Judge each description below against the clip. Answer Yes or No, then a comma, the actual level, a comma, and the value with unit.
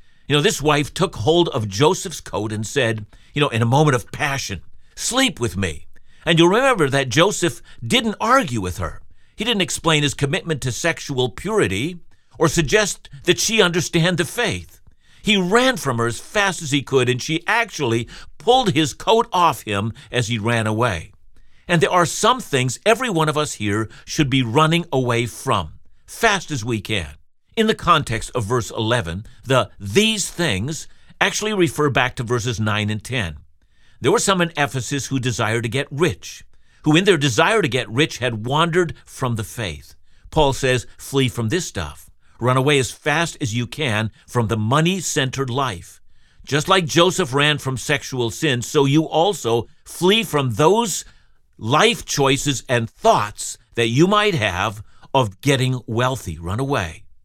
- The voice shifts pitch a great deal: Yes, wide, 6.7 semitones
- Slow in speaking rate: No, average, 175 wpm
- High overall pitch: No, low, 135 Hz